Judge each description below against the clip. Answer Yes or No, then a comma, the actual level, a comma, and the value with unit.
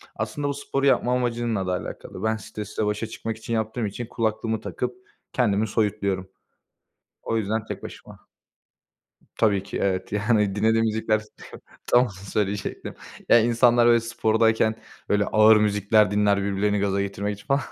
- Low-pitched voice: Yes, low, 110 Hz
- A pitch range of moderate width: No, narrow, 2.0 semitones